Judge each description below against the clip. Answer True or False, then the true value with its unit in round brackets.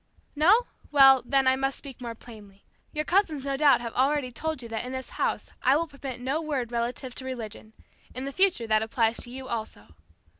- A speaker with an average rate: False (210 wpm)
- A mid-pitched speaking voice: False (260 Hz)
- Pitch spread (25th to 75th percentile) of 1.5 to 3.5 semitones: True (3.2 semitones)